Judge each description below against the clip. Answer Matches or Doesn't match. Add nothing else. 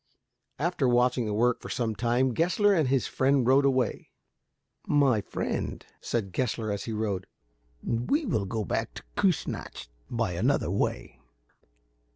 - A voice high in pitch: Doesn't match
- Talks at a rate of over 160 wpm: Doesn't match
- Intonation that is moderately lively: Matches